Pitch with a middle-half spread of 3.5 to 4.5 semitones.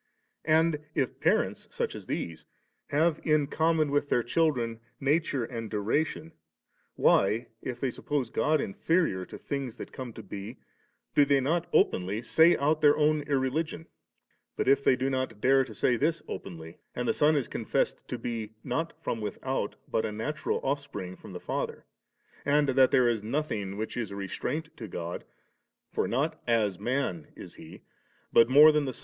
No: average, 5.1 semitones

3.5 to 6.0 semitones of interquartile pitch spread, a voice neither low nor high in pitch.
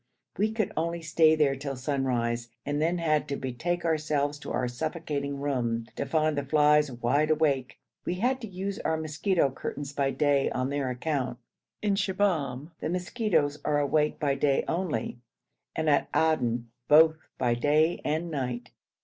No: average, 3.0 semitones; medium, 150 Hz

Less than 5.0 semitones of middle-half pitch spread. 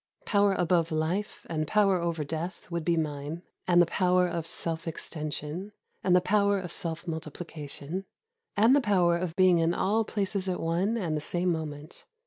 Yes: average, 2.8 semitones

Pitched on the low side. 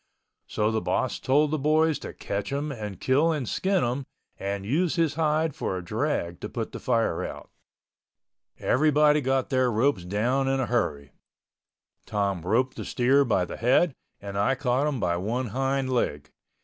Yes: low, 130 Hz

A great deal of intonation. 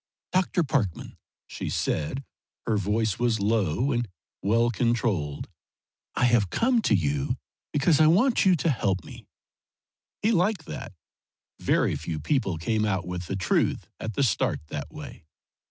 Yes: wide, 7.2 semitones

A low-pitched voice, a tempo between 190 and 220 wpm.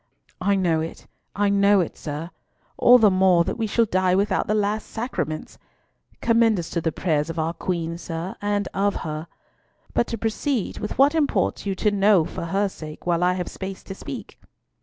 No: high, 190 Hz; average, 195 wpm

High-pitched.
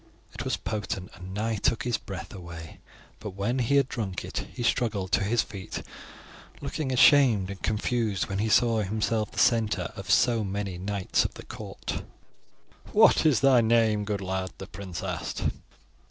No: low, 105 Hz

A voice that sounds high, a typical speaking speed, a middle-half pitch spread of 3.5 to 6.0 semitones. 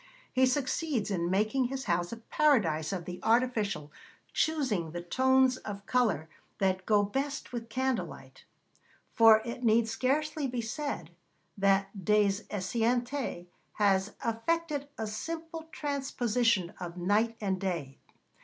No: high, 225 Hz; slow, 130 wpm; average, 5.2 semitones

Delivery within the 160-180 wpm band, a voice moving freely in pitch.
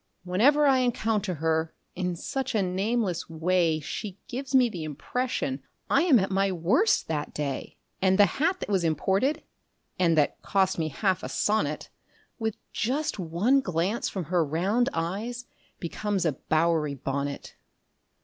No: average, 150 wpm; wide, 6.0 semitones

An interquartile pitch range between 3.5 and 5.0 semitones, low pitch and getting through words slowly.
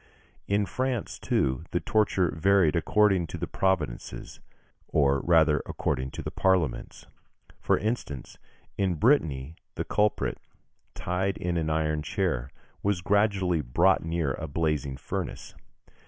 Yes: average, 4.5 semitones; very low, 85 Hz; slow, 125 wpm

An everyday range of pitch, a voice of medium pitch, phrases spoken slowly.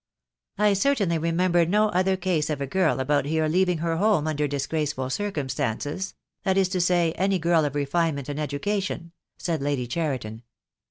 No: average, 4.4 semitones; medium, 165 Hz; average, 170 wpm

